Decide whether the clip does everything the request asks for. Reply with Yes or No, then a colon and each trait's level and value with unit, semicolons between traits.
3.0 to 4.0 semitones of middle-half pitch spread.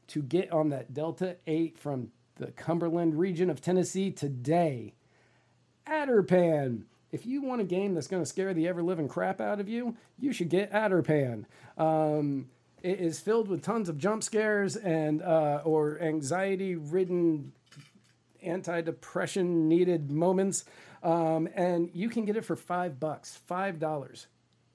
Yes: average, 3.4 semitones